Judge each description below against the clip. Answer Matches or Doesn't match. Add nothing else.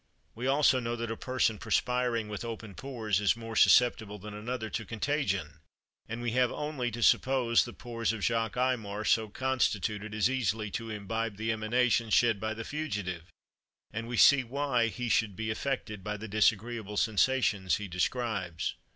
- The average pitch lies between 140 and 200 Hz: Doesn't match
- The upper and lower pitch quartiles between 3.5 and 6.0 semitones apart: Doesn't match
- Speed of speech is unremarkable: Matches